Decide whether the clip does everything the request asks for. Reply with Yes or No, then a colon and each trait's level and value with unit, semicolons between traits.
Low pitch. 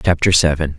Yes: very low, 80 Hz